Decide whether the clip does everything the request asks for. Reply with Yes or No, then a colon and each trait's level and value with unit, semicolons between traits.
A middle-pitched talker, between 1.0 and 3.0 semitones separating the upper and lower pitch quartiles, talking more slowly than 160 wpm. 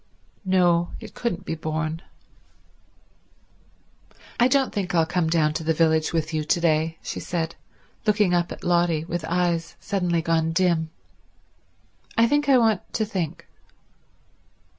Yes: medium, 170 Hz; narrow, 2.5 semitones; average, 140 wpm